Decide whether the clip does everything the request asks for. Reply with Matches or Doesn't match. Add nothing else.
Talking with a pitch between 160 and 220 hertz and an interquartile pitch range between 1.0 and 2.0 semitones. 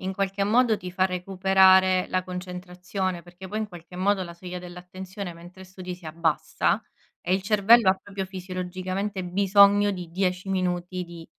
Matches